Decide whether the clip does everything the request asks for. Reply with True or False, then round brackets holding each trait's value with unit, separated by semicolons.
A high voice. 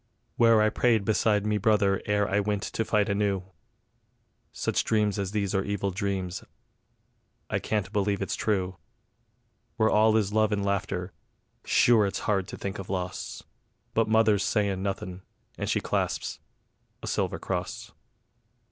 False (100 Hz)